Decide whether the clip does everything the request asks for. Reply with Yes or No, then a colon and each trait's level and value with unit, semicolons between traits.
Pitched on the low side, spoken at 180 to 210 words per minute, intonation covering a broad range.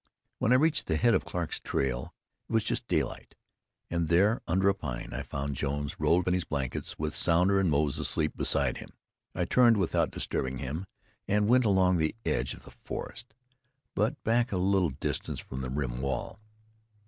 Yes: very low, 85 Hz; average, 185 wpm; wide, 6.1 semitones